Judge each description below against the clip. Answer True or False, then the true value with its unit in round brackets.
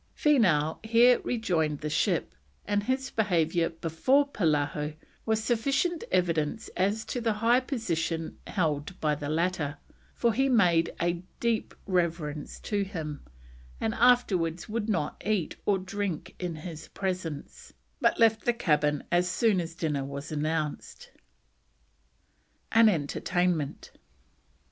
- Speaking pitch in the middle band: True (180 Hz)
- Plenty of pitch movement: True (5.9 semitones)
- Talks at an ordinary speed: False (125 wpm)